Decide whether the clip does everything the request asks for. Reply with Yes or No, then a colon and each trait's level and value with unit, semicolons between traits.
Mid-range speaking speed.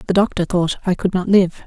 No: fast, 250 wpm